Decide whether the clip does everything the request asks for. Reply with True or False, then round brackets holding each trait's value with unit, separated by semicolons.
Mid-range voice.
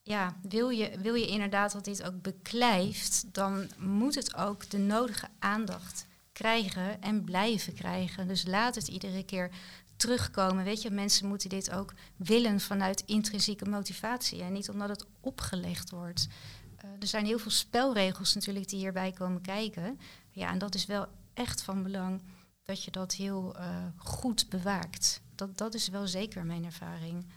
False (195 Hz)